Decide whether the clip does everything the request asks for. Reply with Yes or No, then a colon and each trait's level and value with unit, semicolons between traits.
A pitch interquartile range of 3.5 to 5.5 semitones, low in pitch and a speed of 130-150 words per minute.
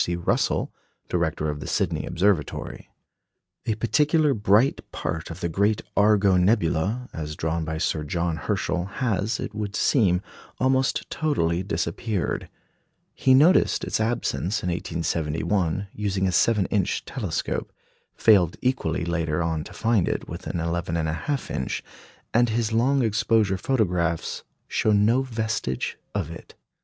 Yes: average, 5.2 semitones; very low, 95 Hz; average, 140 wpm